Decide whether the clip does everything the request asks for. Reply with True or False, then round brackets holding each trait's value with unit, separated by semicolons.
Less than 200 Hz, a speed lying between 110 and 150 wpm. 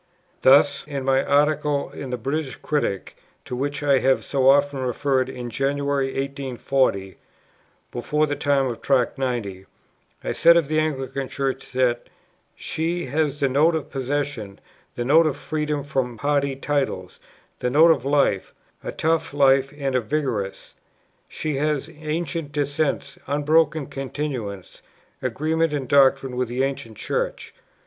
True (140 Hz; 145 wpm)